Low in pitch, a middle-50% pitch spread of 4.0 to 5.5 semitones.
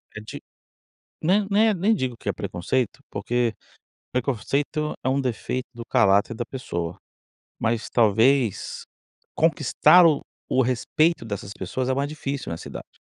Yes: low, 125 Hz; average, 4.4 semitones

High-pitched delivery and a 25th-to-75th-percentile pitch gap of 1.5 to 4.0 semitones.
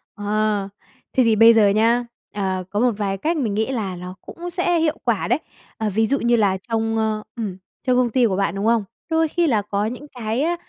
Yes: high, 225 Hz; average, 3.5 semitones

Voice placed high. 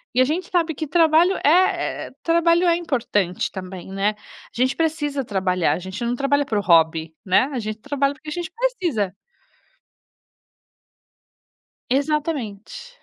Yes: very high, 275 Hz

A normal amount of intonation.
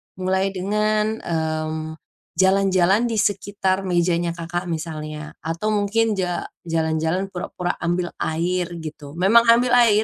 Yes: average, 3.7 semitones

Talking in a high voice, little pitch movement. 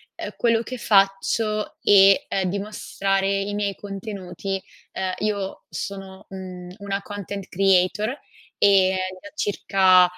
Yes: high, 195 Hz; narrow, 1.3 semitones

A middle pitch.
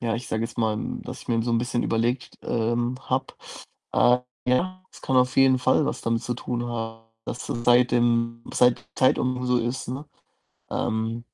No: low, 120 Hz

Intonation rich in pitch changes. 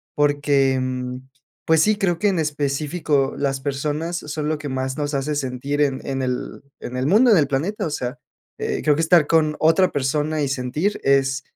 No: average, 2.8 semitones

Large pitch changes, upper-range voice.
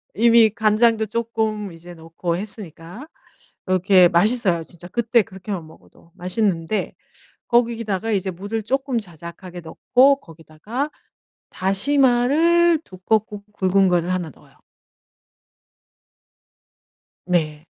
No: average, 4.7 semitones; high, 200 Hz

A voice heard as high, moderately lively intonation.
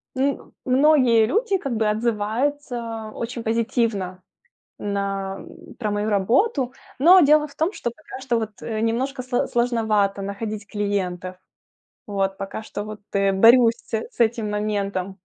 Yes: high, 225 Hz; average, 3.7 semitones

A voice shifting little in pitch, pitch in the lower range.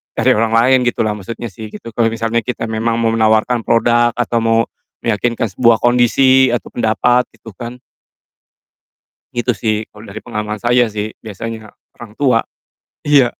Yes: narrow, 1.7 semitones; low, 115 Hz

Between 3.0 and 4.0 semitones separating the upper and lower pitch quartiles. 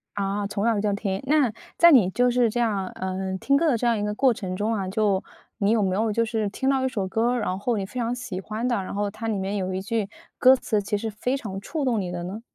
Yes: average, 3.5 semitones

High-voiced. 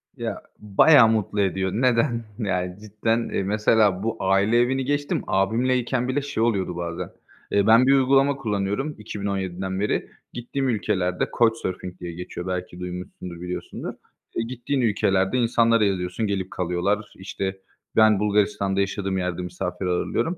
No: low, 105 Hz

